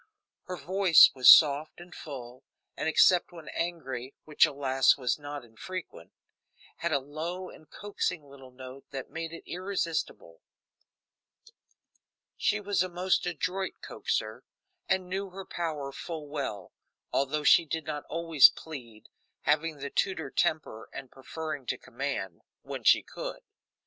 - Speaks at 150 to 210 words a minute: No, average, 140 wpm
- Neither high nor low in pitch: Yes, medium, 155 Hz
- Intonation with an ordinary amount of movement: Yes, average, 4.5 semitones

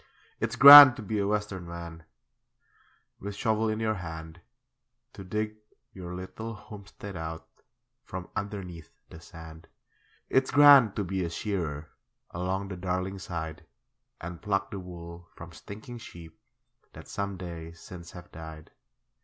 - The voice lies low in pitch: Yes, very low, 95 Hz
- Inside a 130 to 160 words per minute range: Yes, average, 140 wpm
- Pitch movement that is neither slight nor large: Yes, average, 3.7 semitones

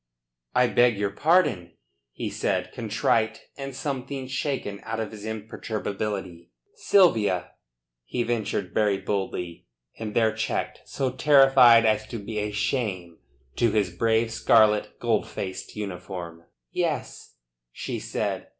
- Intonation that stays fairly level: No, average, 3.3 semitones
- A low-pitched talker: Yes, low, 110 Hz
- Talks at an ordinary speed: No, slow, 125 wpm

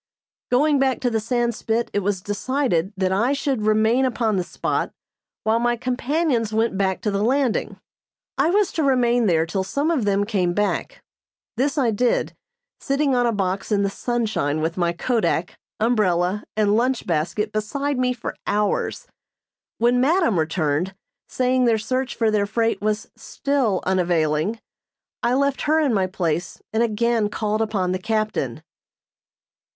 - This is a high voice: Yes, high, 220 Hz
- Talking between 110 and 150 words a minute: No, average, 160 wpm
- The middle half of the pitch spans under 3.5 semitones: No, average, 4.5 semitones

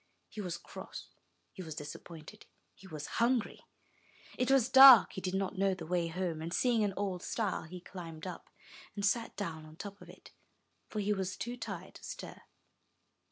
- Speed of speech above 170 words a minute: Yes, average, 190 wpm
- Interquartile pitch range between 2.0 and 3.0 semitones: No, average, 3.9 semitones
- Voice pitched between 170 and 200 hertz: Yes, high, 190 Hz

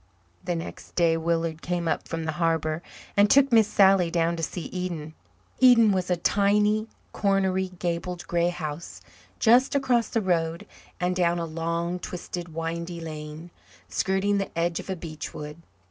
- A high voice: No, medium, 175 Hz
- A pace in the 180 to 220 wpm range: No, average, 160 wpm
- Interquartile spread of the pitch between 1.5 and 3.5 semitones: Yes, average, 2.7 semitones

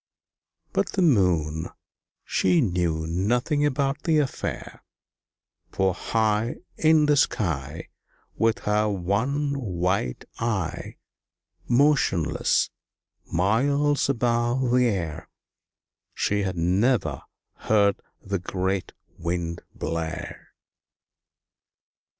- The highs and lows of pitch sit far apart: Yes, wide, 6.5 semitones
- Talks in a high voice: No, low, 105 Hz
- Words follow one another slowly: Yes, slow, 85 wpm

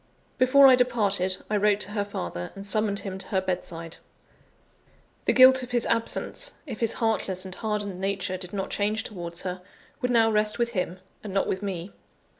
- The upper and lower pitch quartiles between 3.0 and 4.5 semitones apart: Yes, average, 3.4 semitones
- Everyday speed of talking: Yes, average, 190 wpm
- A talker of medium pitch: No, high, 205 Hz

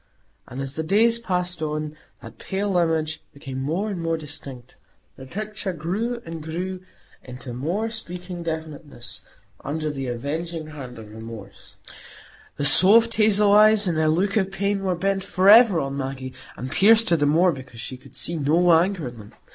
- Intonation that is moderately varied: No, wide, 6.0 semitones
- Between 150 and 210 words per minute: Yes, average, 170 wpm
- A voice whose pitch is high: No, medium, 165 Hz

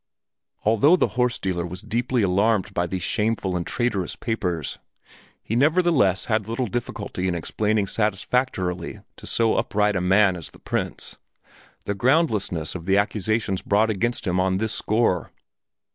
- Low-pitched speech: Yes, low, 105 Hz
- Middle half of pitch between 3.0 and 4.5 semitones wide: Yes, average, 3.9 semitones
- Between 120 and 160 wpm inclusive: Yes, average, 150 wpm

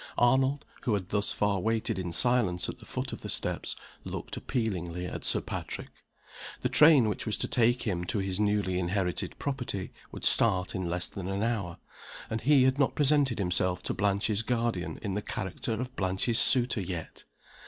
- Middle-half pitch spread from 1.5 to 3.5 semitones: No, average, 4.7 semitones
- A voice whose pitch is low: Yes, low, 105 Hz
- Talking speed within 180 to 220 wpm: Yes, average, 185 wpm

